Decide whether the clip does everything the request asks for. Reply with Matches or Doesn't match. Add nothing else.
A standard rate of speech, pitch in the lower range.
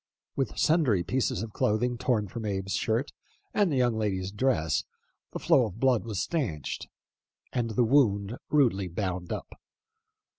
Matches